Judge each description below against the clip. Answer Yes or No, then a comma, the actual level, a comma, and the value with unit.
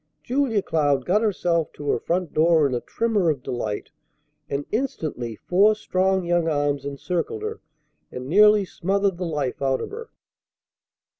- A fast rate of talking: No, average, 155 wpm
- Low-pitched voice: No, medium, 170 Hz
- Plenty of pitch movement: Yes, wide, 6.2 semitones